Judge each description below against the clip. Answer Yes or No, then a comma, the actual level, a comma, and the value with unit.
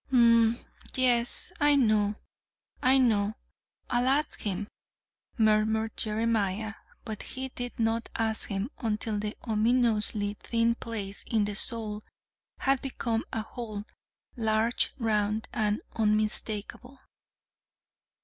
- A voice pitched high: Yes, high, 220 Hz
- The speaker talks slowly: Yes, slow, 110 wpm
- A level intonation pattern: Yes, narrow, 2.1 semitones